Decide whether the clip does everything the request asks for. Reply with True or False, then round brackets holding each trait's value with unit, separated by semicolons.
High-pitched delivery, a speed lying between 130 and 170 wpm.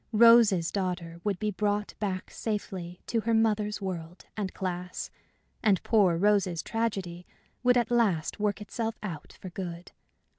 True (200 Hz; 145 wpm)